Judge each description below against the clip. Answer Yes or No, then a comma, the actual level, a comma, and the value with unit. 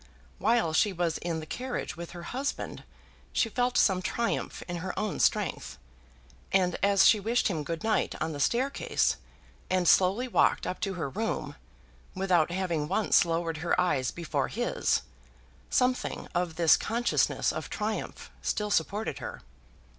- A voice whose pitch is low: No, medium, 185 Hz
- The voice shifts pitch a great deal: No, average, 4.6 semitones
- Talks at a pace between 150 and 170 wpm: Yes, average, 155 wpm